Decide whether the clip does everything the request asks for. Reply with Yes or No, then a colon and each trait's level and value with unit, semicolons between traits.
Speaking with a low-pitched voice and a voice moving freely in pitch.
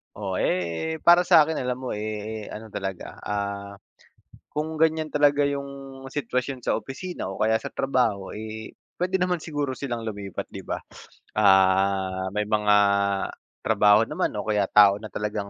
Yes: low, 110 Hz; wide, 5.9 semitones